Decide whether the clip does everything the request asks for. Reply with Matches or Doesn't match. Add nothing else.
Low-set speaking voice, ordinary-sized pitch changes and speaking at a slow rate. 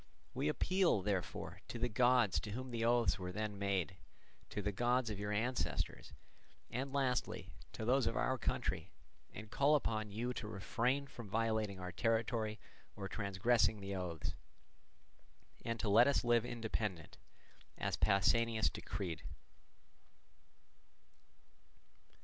Matches